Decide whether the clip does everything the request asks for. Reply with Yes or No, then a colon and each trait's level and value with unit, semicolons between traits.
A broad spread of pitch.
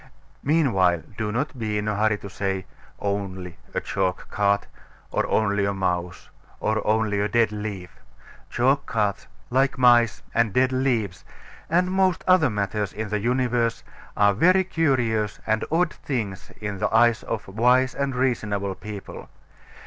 No: average, 4.1 semitones